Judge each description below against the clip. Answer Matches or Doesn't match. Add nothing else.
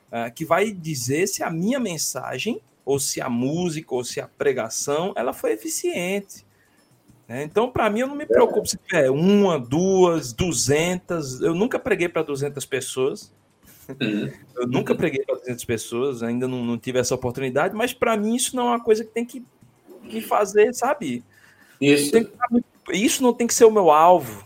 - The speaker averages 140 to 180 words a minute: Matches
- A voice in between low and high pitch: Matches